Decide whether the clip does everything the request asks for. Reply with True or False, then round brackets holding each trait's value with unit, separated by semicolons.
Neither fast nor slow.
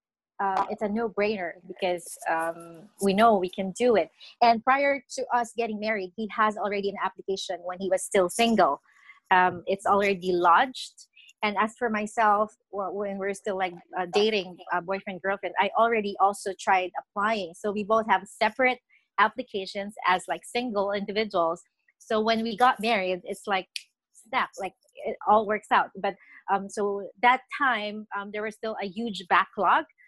True (175 wpm)